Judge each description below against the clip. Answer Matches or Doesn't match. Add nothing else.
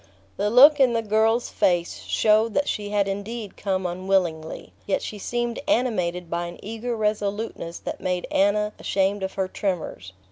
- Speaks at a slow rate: Doesn't match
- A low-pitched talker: Doesn't match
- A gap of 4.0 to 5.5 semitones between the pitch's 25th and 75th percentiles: Doesn't match